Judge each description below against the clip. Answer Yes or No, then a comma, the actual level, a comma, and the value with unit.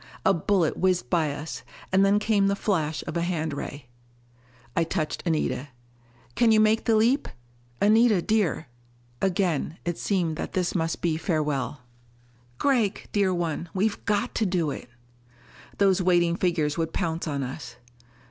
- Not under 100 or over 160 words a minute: Yes, average, 155 wpm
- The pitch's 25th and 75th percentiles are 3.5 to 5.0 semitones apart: Yes, average, 4.1 semitones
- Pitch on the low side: No, medium, 175 Hz